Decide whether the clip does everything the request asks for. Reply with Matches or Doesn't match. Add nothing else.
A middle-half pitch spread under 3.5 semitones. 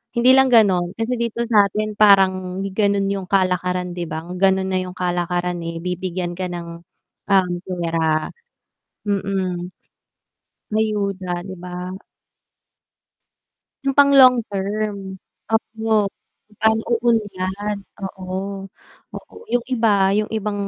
Matches